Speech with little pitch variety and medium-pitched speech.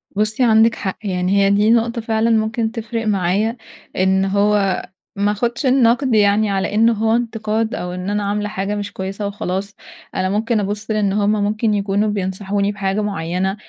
No: narrow, 2.0 semitones; high, 210 Hz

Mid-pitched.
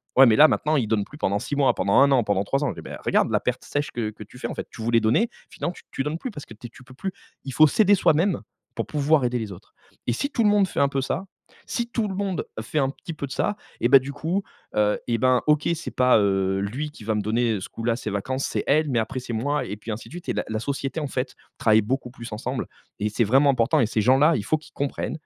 No: low, 130 Hz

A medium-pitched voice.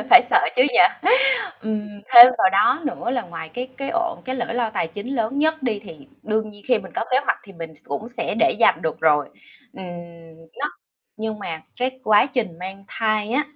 No: high, 220 Hz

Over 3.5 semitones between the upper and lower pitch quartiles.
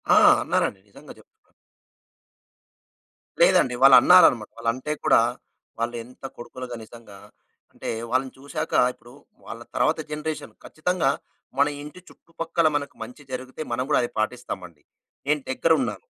Yes: average, 4.5 semitones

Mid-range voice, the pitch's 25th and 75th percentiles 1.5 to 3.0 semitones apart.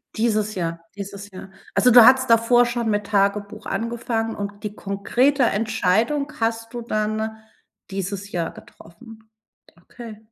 No: high, 220 Hz; narrow, 2.6 semitones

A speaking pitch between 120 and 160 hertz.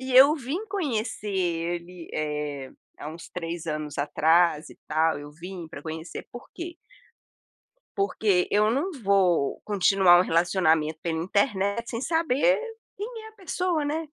No: high, 190 Hz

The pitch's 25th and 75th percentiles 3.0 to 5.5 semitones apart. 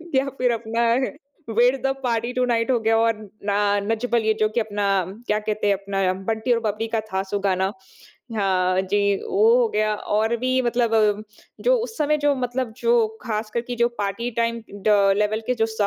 No: narrow, 2.6 semitones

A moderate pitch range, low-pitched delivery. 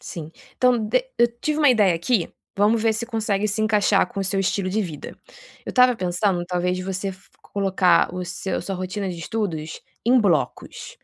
No: average, 3.4 semitones; high, 195 Hz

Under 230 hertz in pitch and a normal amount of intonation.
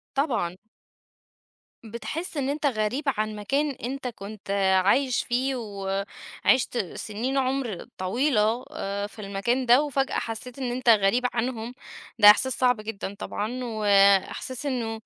No: high, 235 Hz; average, 4.0 semitones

